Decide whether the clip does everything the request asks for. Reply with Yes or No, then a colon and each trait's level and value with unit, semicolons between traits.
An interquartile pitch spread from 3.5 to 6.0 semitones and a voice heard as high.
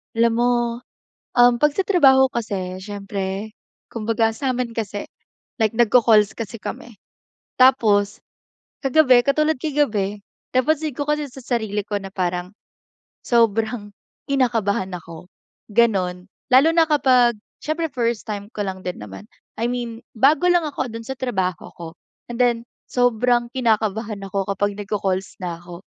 Yes: average, 4.0 semitones; high, 225 Hz